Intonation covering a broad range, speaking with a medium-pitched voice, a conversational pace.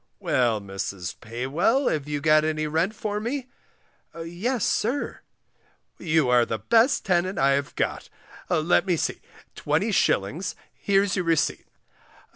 No: wide, 6.4 semitones; medium, 165 Hz; slow, 130 wpm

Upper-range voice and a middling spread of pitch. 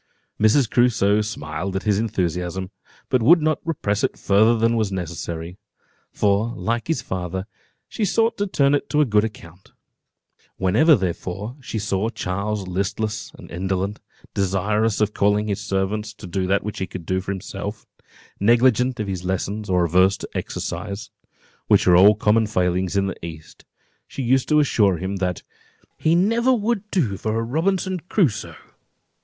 No: low, 105 Hz; average, 3.9 semitones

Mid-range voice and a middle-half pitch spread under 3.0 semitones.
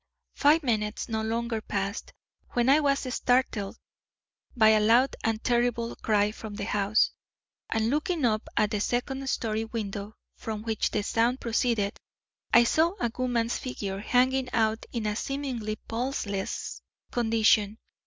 No: high, 225 Hz; narrow, 2.6 semitones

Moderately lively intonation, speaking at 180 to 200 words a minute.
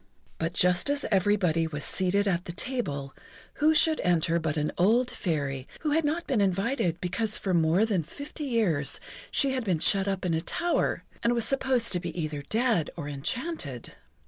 No: wide, 7.0 semitones; average, 185 wpm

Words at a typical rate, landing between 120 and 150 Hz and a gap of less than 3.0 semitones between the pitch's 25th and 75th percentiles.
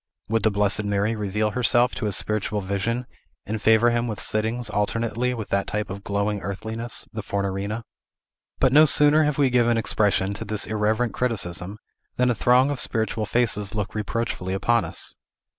No: average, 175 wpm; low, 110 Hz; narrow, 2.6 semitones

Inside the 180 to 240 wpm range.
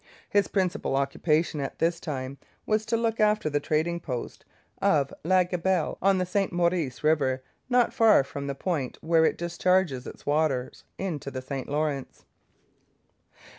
No: average, 155 wpm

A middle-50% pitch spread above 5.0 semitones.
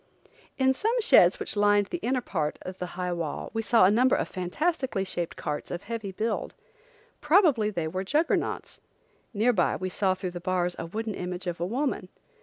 Yes: wide, 5.6 semitones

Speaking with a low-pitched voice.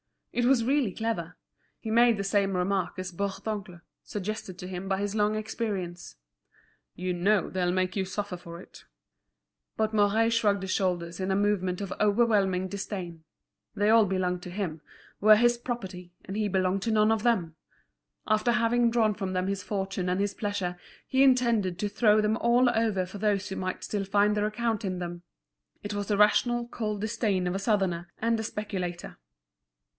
No: high, 200 Hz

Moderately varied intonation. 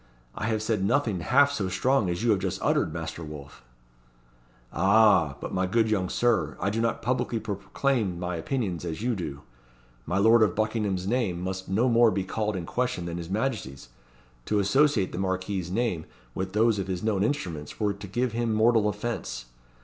Yes: average, 4.0 semitones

